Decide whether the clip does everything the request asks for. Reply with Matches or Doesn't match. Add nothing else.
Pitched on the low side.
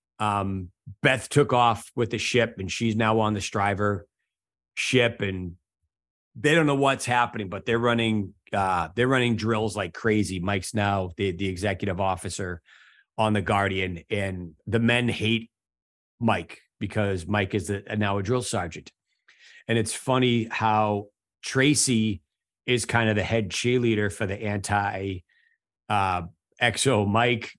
Matches